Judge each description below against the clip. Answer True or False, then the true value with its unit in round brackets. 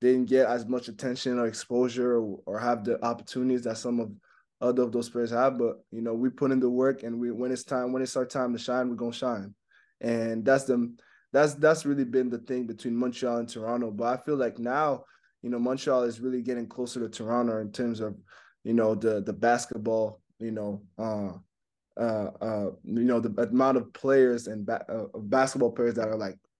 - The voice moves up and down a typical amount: False (1.9 semitones)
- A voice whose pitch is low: True (120 Hz)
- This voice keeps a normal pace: False (220 wpm)